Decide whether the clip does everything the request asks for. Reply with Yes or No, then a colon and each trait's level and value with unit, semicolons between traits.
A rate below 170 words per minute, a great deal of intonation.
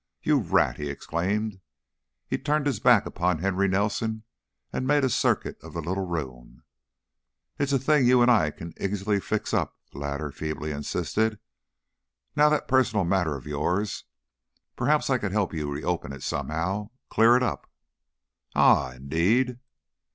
Yes: average, 155 wpm; wide, 7.5 semitones